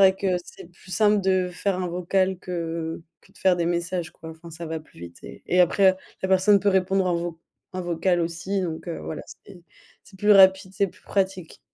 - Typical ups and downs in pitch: No, narrow, 2.1 semitones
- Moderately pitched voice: Yes, medium, 180 Hz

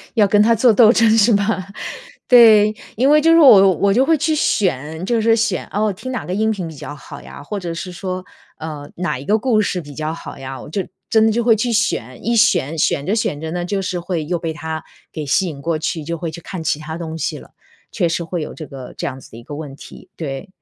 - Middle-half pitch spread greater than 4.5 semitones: Yes, wide, 5.6 semitones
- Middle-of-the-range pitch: Yes, medium, 180 Hz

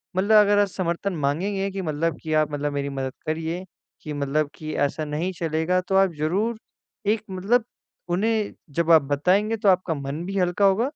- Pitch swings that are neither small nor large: Yes, average, 4.4 semitones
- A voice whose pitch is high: No, medium, 175 Hz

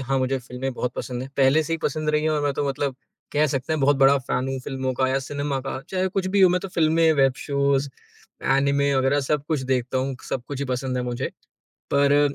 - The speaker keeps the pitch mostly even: Yes, narrow, 2.1 semitones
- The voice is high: No, medium, 140 Hz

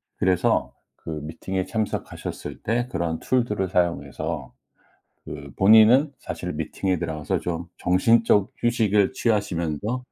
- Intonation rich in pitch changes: No, average, 5.0 semitones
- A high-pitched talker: No, very low, 95 Hz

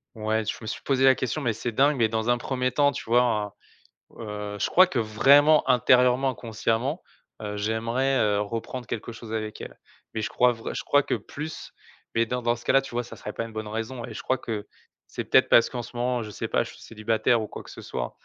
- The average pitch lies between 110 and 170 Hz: Yes, low, 115 Hz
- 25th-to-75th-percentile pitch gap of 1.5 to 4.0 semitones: Yes, average, 2.7 semitones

